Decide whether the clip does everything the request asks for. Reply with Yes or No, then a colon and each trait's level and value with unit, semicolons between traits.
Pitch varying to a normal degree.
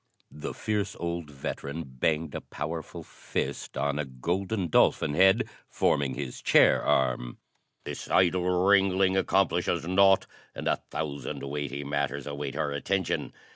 Yes: average, 4.7 semitones